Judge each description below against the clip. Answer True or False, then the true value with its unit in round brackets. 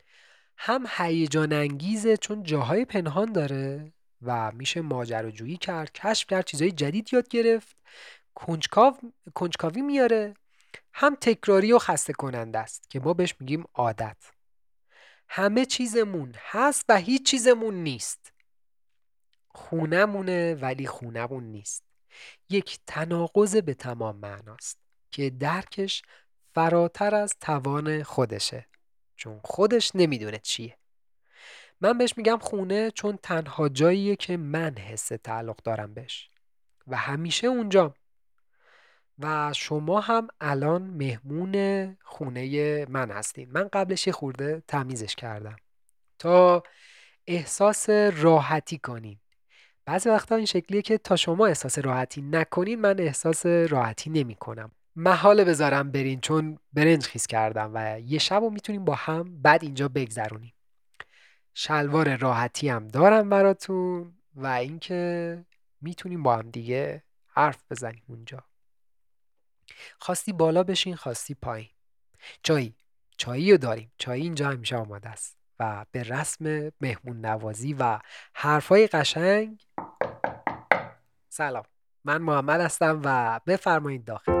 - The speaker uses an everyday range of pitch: False (7.4 semitones)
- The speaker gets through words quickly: False (115 wpm)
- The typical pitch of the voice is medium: True (155 Hz)